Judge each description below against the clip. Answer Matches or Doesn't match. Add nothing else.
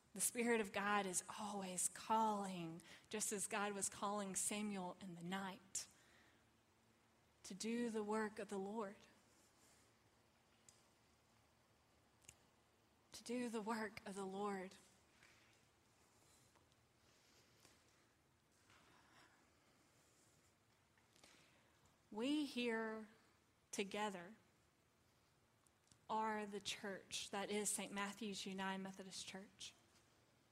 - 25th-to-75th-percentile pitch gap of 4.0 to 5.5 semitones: Matches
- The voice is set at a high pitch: Matches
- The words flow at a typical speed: Doesn't match